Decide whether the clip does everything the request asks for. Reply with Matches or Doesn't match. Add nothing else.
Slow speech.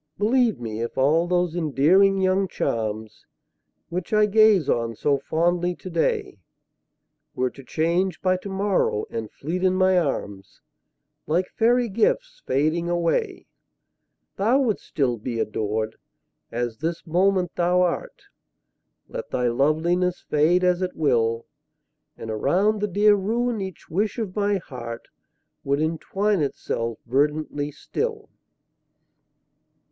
Matches